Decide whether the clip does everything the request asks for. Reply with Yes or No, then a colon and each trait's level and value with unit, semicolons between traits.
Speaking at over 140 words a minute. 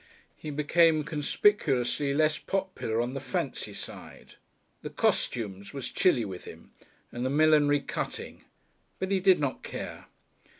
No: slow, 135 wpm